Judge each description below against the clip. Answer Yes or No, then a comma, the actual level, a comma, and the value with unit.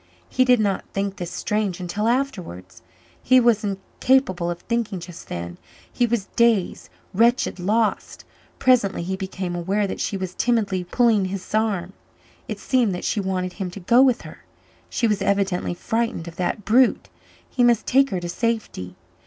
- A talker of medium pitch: No, high, 200 Hz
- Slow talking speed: No, average, 170 wpm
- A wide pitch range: No, average, 4.3 semitones